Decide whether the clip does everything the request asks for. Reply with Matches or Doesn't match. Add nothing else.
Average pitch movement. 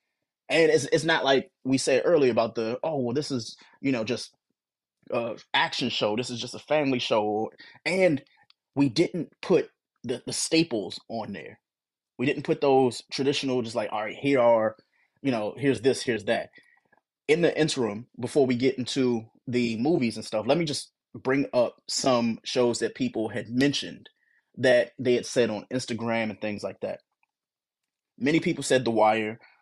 Matches